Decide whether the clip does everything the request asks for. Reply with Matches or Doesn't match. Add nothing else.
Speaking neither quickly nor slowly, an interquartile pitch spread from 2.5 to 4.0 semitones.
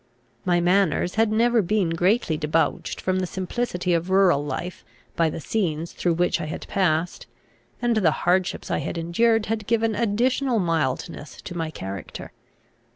Doesn't match